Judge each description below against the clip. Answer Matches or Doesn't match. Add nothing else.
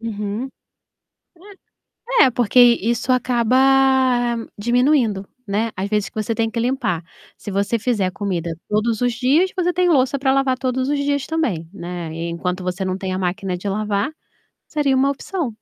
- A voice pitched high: Matches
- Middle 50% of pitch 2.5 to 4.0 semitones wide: Doesn't match